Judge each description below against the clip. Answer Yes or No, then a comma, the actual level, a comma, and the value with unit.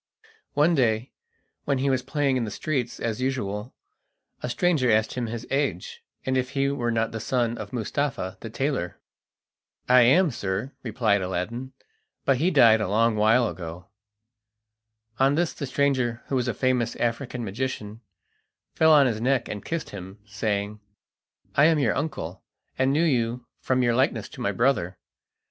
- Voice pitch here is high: No, low, 125 Hz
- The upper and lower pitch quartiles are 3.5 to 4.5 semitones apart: Yes, average, 3.9 semitones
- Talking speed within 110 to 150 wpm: No, average, 165 wpm